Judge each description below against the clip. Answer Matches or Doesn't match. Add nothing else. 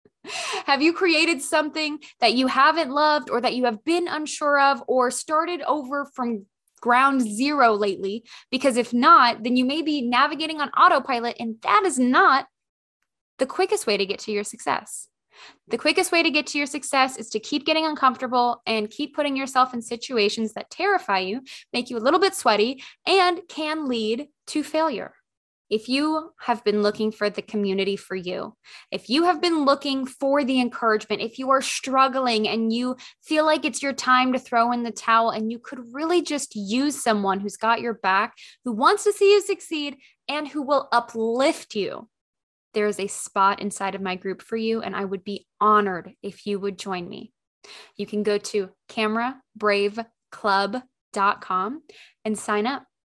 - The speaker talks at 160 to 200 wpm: Matches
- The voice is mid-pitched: Doesn't match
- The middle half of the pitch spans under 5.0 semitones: Doesn't match